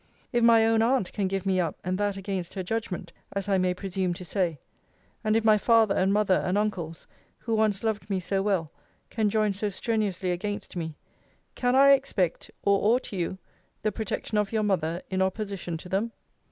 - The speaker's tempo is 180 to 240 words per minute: Yes, average, 195 wpm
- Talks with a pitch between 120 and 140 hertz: No, high, 200 Hz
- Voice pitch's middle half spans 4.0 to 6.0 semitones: No, average, 2.8 semitones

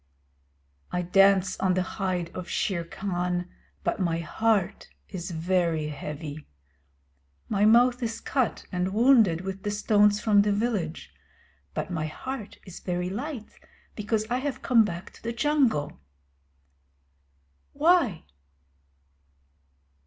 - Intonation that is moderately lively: Yes, average, 4.3 semitones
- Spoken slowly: Yes, slow, 125 wpm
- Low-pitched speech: No, high, 195 Hz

